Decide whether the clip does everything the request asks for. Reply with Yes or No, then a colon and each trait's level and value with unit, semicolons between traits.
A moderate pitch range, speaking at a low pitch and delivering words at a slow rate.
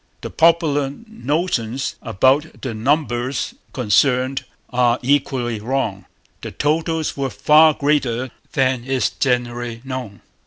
Yes: average, 3.3 semitones; low, 130 Hz; slow, 110 wpm